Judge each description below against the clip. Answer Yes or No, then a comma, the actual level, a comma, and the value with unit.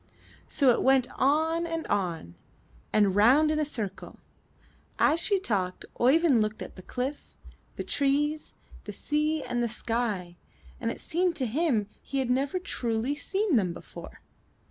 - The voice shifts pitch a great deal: Yes, wide, 6.0 semitones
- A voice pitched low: No, very high, 265 Hz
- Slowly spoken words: No, average, 155 wpm